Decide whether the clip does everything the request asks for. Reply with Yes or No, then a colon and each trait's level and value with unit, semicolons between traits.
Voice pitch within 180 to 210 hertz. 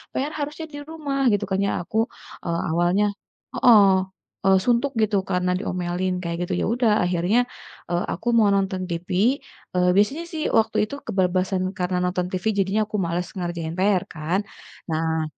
Yes: medium, 185 Hz